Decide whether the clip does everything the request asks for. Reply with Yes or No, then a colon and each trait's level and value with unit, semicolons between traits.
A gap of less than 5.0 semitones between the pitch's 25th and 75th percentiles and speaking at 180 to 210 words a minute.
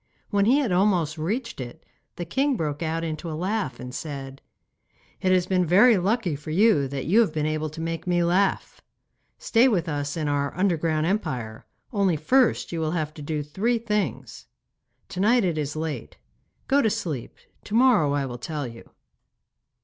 No: wide, 5.4 semitones; average, 185 wpm